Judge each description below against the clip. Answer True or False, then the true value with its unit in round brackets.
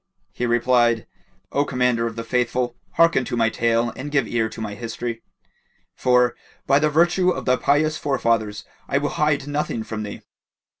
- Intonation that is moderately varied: True (3.6 semitones)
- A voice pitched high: False (125 Hz)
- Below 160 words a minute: False (170 wpm)